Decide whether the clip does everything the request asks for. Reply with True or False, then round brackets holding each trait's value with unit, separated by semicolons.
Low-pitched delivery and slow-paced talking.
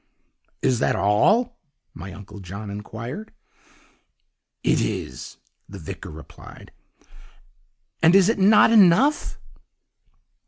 True (130 Hz; 95 wpm)